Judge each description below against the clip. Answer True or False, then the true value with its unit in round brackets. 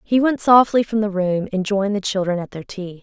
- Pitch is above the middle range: True (200 Hz)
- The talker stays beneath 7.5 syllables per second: True (5.6 syllables/s)